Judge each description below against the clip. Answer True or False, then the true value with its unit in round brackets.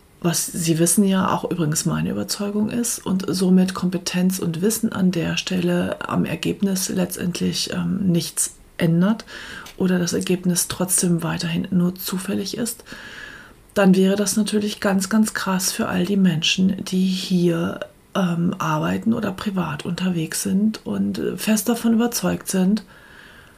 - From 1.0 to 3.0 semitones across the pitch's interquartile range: True (2.6 semitones)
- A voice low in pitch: False (185 Hz)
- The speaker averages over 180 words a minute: False (140 wpm)